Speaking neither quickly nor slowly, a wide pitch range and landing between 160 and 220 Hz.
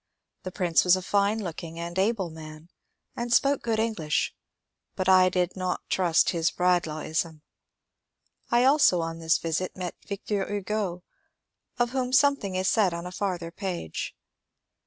No: average, 155 wpm; average, 3.6 semitones; medium, 185 Hz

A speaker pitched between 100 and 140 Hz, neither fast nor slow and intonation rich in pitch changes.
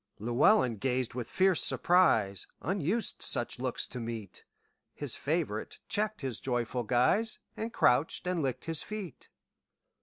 No: low, 135 Hz; slow, 115 wpm; wide, 7.6 semitones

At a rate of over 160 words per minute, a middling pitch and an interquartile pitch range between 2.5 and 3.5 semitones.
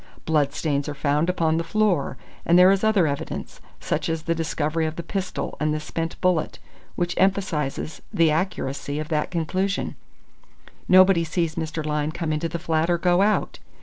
Yes: average, 175 wpm; medium, 165 Hz; average, 2.9 semitones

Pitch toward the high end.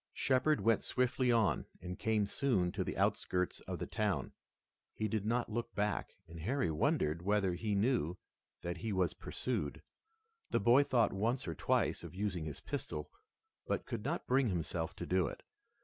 No: low, 105 Hz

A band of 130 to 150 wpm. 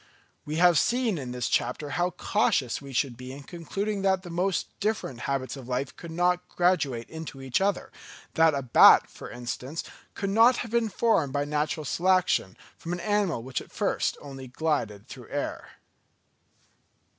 No: average, 175 wpm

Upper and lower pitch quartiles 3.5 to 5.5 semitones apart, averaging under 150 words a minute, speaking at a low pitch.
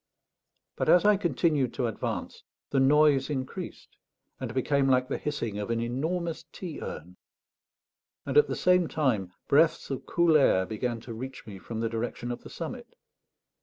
No: average, 4.7 semitones; average, 165 wpm; low, 130 Hz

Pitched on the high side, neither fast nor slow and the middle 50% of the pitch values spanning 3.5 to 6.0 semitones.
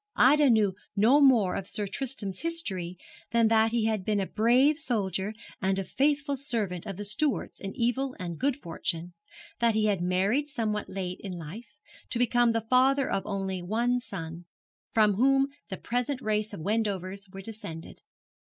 Yes: high, 215 Hz; average, 170 wpm; average, 4.5 semitones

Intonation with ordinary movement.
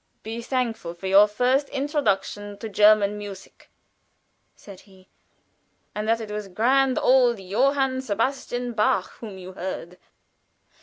Yes: average, 4.2 semitones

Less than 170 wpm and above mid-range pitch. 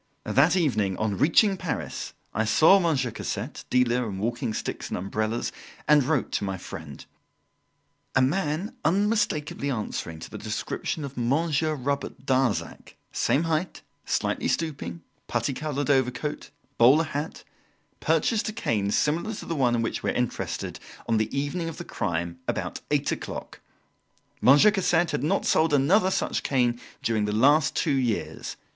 No: average, 155 wpm; medium, 140 Hz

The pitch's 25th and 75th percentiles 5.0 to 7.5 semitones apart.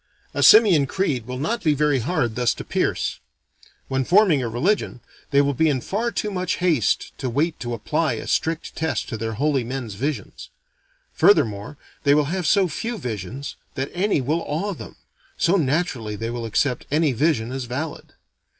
Yes: wide, 5.6 semitones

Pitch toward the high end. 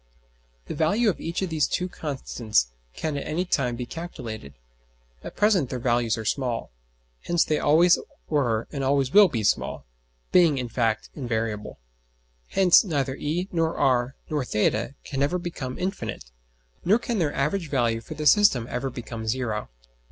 No: medium, 140 Hz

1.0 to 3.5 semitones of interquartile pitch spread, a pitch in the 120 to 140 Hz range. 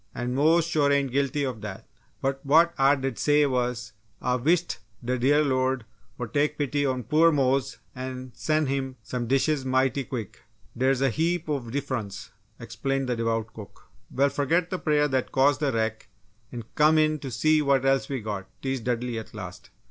Yes: average, 2.9 semitones; low, 135 Hz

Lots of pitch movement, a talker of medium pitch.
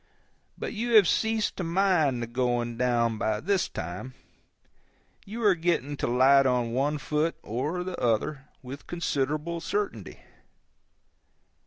Yes: wide, 6.4 semitones; medium, 145 Hz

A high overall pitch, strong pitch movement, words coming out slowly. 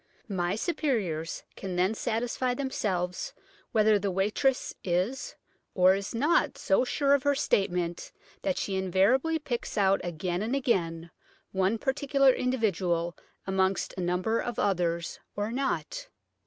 Yes: high, 200 Hz; wide, 6.2 semitones; slow, 130 wpm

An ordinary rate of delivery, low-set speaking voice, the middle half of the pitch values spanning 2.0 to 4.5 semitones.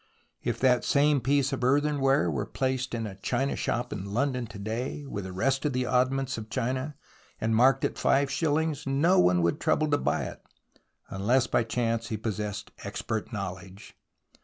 Yes: average, 185 wpm; low, 125 Hz; average, 4.0 semitones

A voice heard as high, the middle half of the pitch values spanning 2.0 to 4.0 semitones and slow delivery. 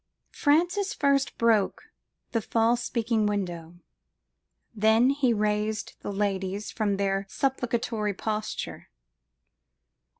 Yes: high, 220 Hz; average, 3.2 semitones; slow, 95 wpm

